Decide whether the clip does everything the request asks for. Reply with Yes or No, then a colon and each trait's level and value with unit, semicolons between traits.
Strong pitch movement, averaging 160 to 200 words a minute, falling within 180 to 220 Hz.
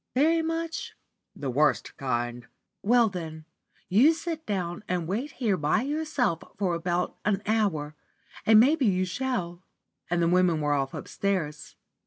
No: wide, 7.3 semitones; average, 145 wpm; medium, 185 Hz